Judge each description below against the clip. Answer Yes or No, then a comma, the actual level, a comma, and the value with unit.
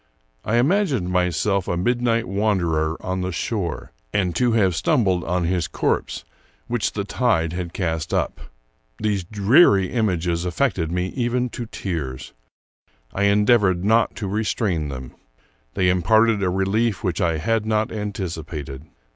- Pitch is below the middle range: Yes, very low, 95 Hz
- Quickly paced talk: No, average, 145 wpm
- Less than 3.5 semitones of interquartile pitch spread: No, average, 4.3 semitones